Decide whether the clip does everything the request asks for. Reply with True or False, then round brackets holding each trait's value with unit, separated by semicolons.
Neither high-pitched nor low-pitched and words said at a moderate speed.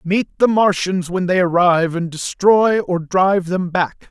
True (180 Hz; 175 wpm)